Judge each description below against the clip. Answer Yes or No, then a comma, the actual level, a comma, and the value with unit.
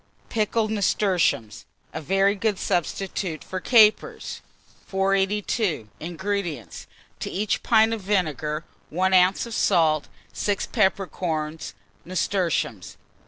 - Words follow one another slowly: Yes, slow, 100 wpm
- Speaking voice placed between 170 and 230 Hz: Yes, high, 190 Hz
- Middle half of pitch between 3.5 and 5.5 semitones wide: Yes, average, 4.1 semitones